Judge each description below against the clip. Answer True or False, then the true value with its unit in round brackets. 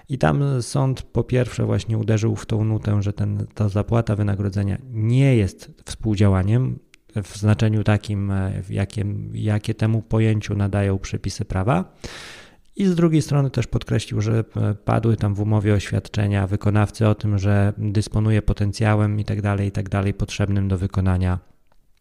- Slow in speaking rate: False (140 wpm)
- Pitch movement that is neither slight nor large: False (1.7 semitones)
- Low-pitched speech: True (105 Hz)